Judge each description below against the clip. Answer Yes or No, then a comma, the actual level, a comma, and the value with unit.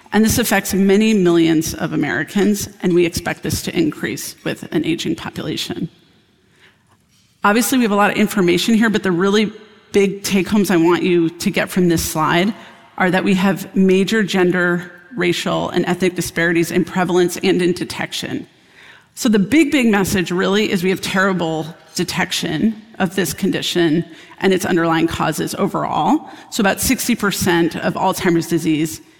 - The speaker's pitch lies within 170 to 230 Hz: Yes, medium, 185 Hz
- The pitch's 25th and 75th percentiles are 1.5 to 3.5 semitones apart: Yes, narrow, 2.6 semitones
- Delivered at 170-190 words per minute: No, average, 160 wpm